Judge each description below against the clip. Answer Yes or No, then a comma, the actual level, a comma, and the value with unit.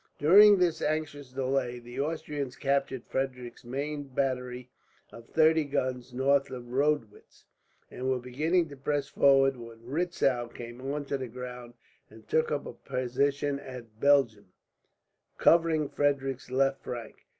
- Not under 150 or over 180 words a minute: No, slow, 135 wpm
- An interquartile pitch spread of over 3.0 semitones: No, narrow, 2.6 semitones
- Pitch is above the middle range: No, low, 135 Hz